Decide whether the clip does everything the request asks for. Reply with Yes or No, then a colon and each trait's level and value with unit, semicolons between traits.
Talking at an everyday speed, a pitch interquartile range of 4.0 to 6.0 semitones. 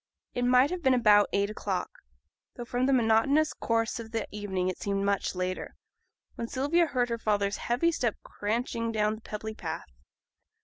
No: average, 175 wpm; average, 3.3 semitones